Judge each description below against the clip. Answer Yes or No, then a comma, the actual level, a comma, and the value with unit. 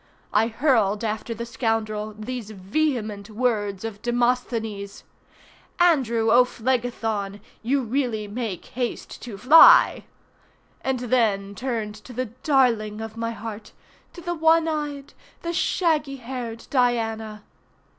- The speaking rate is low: Yes, slow, 115 wpm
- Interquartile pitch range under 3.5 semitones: Yes, average, 3.1 semitones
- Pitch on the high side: Yes, high, 230 Hz